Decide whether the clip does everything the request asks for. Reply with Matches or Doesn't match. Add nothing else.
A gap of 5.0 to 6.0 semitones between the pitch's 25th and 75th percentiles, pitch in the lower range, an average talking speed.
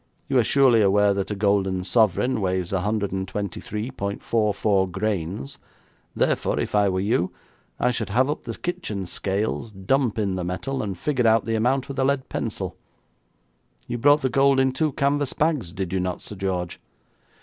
Matches